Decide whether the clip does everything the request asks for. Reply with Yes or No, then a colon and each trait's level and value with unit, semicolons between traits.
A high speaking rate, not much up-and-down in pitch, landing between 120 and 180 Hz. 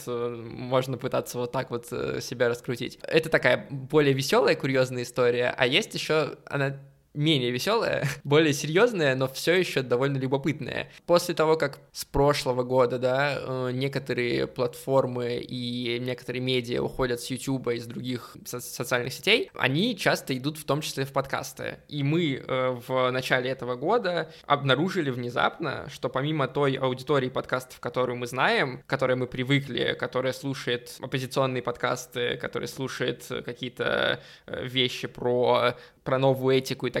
No: average, 145 wpm; narrow, 2.0 semitones; low, 130 Hz